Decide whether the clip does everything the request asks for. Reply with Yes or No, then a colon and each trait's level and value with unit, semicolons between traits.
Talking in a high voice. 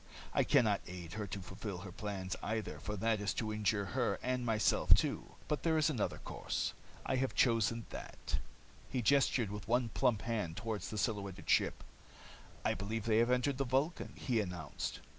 No: low, 110 Hz